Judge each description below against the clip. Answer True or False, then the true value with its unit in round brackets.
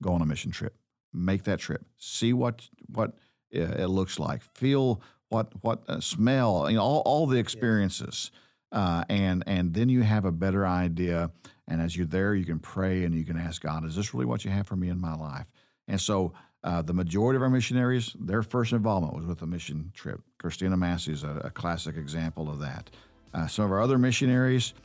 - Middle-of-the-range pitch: False (95 Hz)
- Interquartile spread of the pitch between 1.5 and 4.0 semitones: False (5.3 semitones)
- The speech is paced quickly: True (210 wpm)